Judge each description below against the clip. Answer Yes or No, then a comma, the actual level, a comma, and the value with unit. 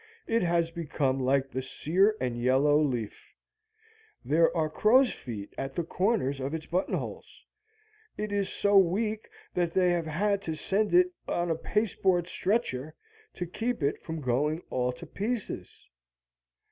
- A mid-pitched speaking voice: Yes, medium, 170 Hz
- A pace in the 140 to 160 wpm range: Yes, average, 155 wpm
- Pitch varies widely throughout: Yes, wide, 6.4 semitones